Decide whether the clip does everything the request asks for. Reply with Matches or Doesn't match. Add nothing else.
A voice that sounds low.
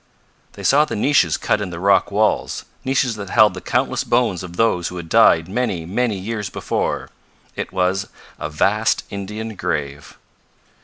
Matches